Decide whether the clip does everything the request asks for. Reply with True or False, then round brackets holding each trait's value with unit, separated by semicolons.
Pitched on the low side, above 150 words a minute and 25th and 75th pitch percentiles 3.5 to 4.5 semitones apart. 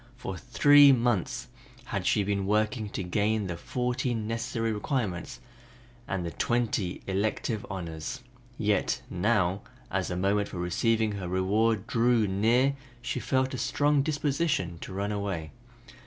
False (105 Hz; 140 wpm; 4.2 semitones)